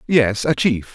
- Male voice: Yes, male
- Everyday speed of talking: Yes, average, 190 wpm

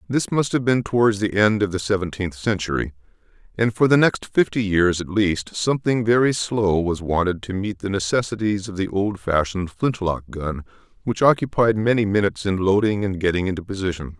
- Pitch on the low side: Yes, low, 100 Hz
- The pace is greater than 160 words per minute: Yes, average, 180 wpm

